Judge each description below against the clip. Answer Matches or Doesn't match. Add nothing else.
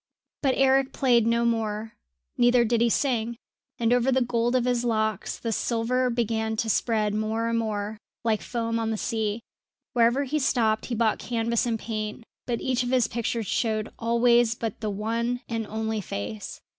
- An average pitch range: Doesn't match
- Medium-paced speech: Matches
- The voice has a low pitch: Doesn't match